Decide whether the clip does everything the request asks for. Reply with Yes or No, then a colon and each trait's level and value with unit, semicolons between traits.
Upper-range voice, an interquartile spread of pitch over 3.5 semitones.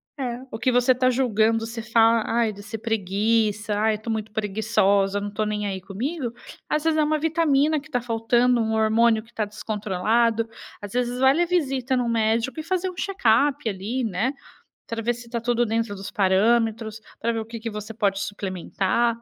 No: high, 225 Hz; narrow, 2.6 semitones